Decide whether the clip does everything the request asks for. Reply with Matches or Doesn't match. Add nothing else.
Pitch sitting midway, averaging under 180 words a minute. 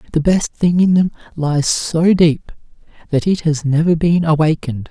Matches